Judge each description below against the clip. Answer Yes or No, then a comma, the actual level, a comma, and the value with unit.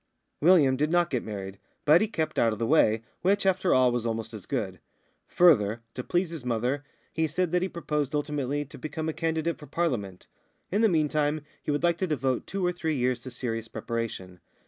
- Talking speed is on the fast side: Yes, fast, 210 wpm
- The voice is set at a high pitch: No, medium, 145 Hz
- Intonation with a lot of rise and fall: Yes, wide, 6.1 semitones